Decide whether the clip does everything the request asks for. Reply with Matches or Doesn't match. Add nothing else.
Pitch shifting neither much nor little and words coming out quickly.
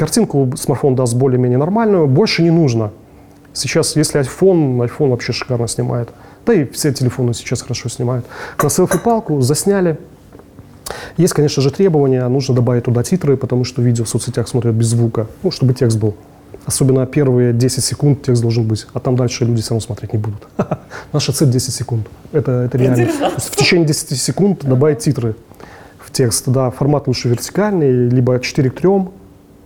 Matches